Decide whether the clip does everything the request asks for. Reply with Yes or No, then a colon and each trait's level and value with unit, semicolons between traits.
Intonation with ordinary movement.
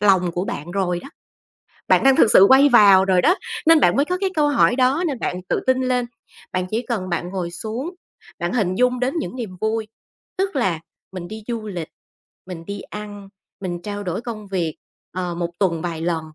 No: wide, 5.8 semitones